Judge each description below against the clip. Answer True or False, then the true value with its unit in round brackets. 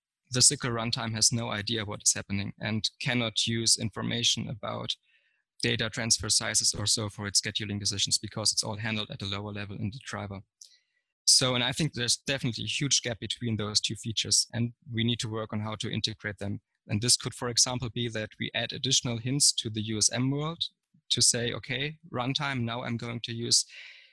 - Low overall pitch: True (115 Hz)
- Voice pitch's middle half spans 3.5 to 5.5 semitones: False (2.7 semitones)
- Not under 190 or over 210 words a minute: True (200 wpm)